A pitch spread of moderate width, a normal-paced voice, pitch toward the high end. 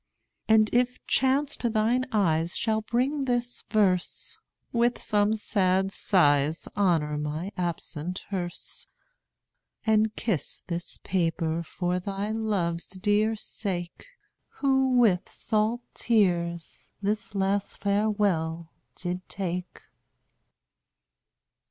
No: average, 4.1 semitones; slow, 100 wpm; high, 195 Hz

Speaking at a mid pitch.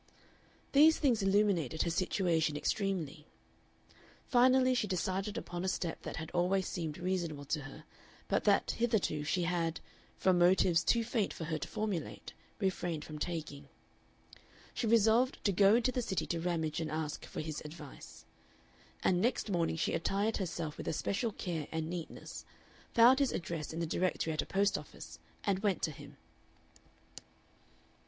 Yes: medium, 180 Hz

